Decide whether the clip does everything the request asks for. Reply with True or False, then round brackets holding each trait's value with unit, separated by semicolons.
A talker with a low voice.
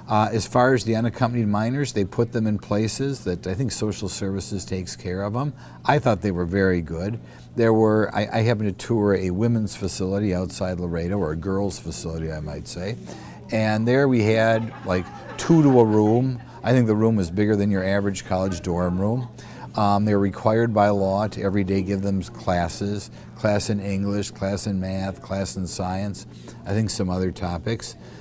True (100 Hz)